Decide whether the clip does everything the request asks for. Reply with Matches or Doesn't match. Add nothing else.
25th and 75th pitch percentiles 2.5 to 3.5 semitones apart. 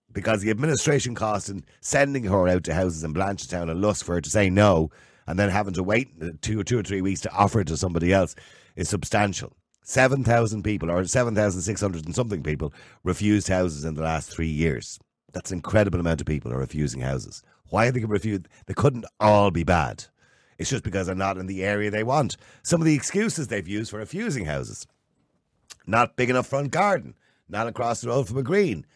Doesn't match